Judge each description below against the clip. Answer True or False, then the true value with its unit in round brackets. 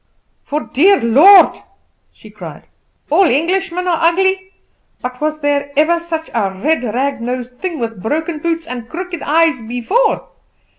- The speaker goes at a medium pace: True (145 wpm)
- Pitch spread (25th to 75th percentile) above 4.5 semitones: True (5.4 semitones)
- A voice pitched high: True (310 Hz)